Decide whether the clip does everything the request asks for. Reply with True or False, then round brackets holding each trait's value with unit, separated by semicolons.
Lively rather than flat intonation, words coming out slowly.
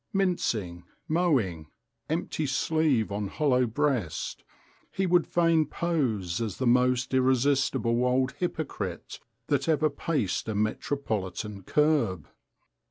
True (6.5 semitones; 105 wpm)